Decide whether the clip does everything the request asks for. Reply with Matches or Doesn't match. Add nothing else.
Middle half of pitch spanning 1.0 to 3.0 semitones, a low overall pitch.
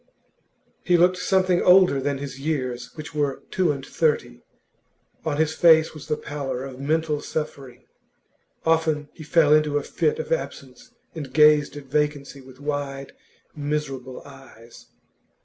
Doesn't match